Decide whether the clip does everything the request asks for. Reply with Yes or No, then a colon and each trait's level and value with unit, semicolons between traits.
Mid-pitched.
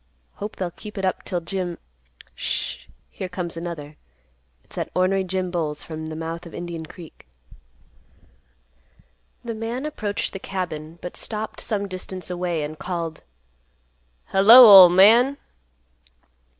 Yes: medium, 180 Hz